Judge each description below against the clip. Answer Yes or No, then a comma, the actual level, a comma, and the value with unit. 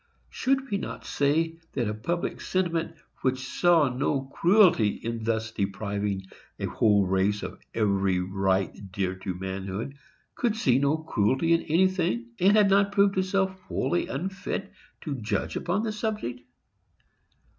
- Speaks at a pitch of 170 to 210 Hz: No, low, 135 Hz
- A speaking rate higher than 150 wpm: No, average, 140 wpm